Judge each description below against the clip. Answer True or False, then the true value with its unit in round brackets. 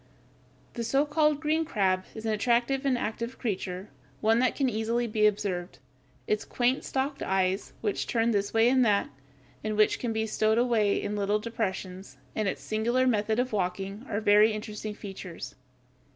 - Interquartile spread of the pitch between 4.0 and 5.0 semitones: False (3.0 semitones)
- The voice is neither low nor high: False (220 Hz)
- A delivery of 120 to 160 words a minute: False (180 wpm)